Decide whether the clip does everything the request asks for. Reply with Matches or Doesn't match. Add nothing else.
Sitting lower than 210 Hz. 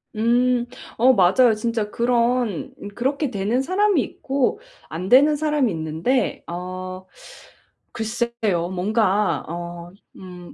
Doesn't match